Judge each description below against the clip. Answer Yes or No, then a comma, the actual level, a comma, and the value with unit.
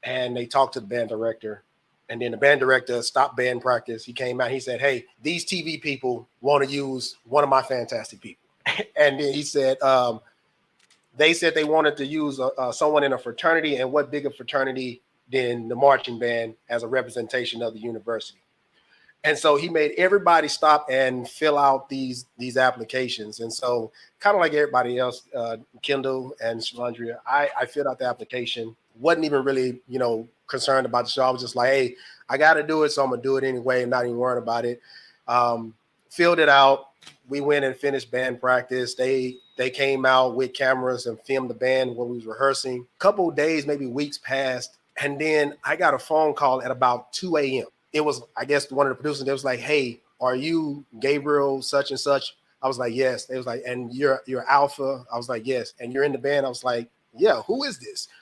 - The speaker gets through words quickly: Yes, fast, 215 wpm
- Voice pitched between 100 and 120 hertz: No, low, 130 Hz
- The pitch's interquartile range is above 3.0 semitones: No, average, 2.7 semitones